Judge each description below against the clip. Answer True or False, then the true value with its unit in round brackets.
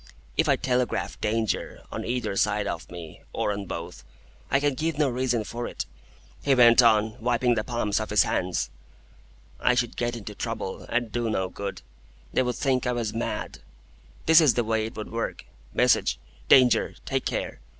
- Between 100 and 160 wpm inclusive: False (180 wpm)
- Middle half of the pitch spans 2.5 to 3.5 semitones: True (2.9 semitones)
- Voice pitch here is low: True (115 Hz)